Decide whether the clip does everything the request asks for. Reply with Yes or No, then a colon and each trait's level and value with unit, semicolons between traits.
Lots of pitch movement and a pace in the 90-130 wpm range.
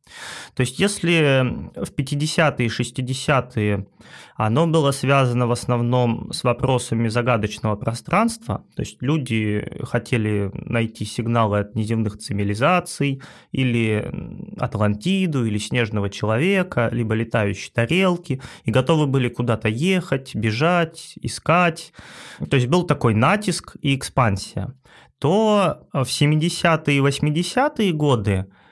Yes: wide, 5.9 semitones; slow, 110 wpm